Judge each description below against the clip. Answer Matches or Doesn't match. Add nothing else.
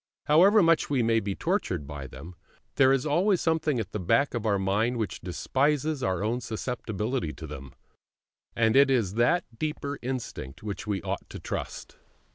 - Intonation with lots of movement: Matches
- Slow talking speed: Doesn't match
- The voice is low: Matches